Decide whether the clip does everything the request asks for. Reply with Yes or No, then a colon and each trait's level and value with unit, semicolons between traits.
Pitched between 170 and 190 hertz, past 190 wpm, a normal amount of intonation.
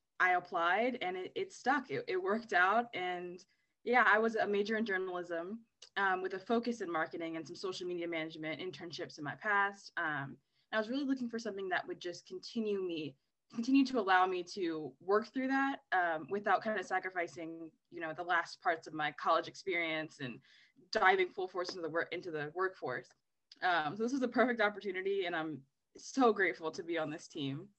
No: medium, 185 Hz; average, 200 wpm; wide, 5.7 semitones